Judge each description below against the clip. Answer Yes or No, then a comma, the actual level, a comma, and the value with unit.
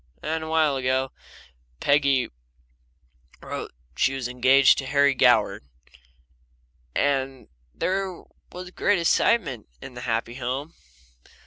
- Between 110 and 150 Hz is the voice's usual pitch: Yes, low, 135 Hz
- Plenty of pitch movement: No, average, 3.5 semitones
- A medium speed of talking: No, slow, 110 wpm